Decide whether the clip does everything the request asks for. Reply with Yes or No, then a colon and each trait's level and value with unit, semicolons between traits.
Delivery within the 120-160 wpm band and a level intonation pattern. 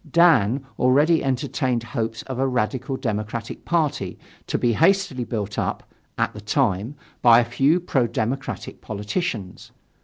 No: average, 140 wpm; average, 4.0 semitones